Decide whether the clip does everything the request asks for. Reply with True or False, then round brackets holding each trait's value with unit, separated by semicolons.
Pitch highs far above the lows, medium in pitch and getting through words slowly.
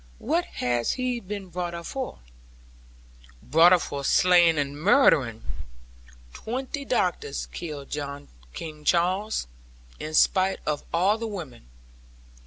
True (5.7 semitones; 175 Hz; 115 wpm)